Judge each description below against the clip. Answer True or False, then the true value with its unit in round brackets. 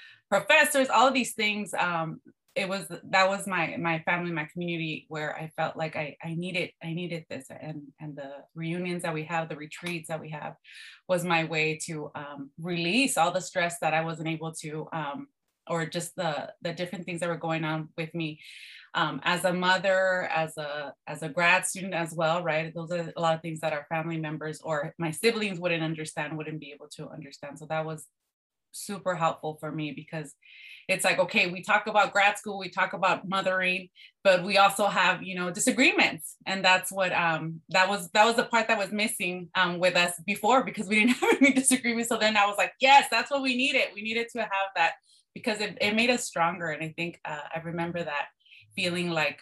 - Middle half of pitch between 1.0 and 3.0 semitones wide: False (3.8 semitones)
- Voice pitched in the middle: True (175 Hz)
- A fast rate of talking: True (215 wpm)